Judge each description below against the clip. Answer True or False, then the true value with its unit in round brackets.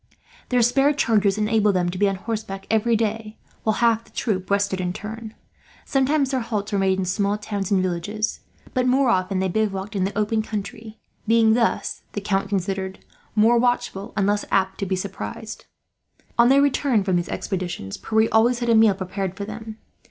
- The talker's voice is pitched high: True (210 Hz)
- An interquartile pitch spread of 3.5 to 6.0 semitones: False (2.8 semitones)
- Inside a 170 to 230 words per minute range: True (190 wpm)